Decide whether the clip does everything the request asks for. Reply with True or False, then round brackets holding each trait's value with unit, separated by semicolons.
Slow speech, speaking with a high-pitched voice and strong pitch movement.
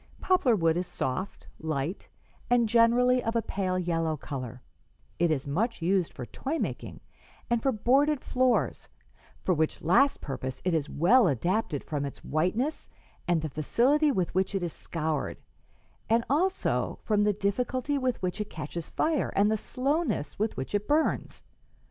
False (160 wpm; 200 Hz; 7.6 semitones)